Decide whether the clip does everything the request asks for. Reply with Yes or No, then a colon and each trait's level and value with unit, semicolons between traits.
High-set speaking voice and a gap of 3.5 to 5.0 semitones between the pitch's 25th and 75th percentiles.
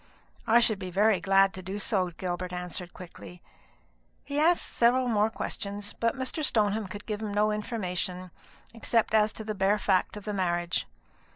No: high, 205 Hz; average, 3.1 semitones